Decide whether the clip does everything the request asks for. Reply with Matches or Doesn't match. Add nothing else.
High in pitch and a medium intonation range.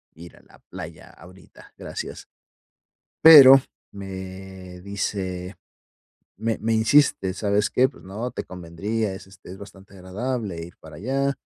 Doesn't match